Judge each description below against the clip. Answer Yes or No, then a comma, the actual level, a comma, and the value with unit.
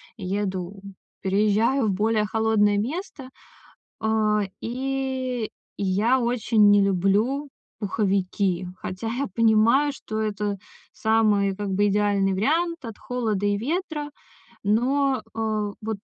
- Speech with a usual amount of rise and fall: Yes, average, 3.6 semitones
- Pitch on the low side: No, high, 215 Hz